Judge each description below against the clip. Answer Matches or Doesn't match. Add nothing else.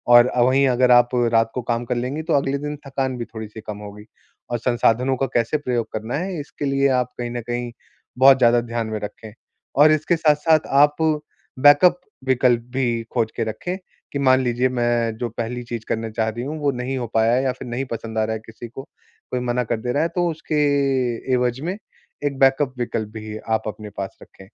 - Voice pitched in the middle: Doesn't match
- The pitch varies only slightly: Doesn't match